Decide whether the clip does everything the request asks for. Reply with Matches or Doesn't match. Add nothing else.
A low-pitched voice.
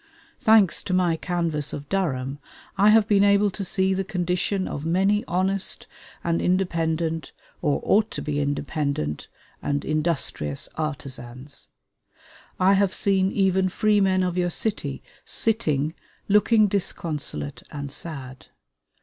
Doesn't match